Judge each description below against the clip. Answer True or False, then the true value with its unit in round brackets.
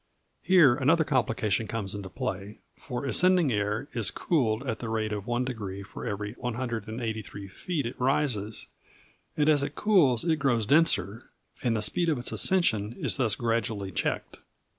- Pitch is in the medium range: False (115 Hz)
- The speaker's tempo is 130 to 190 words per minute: True (160 wpm)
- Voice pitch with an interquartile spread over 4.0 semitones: True (4.9 semitones)